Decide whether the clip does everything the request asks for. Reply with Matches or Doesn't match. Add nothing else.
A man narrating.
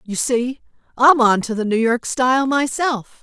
Doesn't match